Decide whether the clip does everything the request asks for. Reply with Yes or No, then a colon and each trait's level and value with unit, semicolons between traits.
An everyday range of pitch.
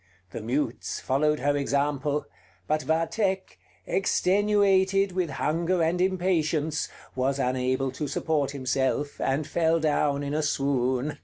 Yes: average, 3.9 semitones